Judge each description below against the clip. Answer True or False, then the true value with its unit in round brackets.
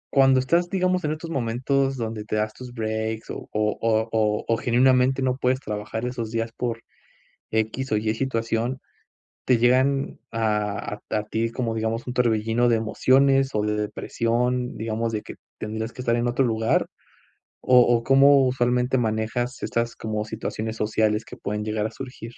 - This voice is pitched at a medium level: False (115 Hz)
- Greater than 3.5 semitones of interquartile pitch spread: False (2.6 semitones)